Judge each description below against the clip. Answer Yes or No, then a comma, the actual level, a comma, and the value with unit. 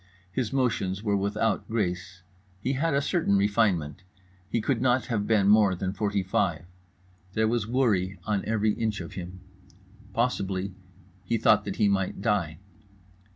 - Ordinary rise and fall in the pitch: Yes, average, 3.1 semitones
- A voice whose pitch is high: No, low, 105 Hz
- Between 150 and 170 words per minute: Yes, average, 155 wpm